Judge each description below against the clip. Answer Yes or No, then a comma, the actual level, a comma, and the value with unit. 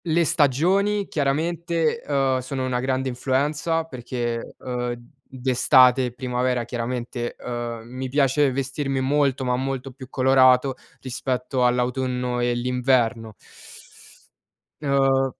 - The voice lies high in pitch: No, low, 130 Hz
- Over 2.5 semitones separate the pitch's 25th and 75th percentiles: No, narrow, 1.8 semitones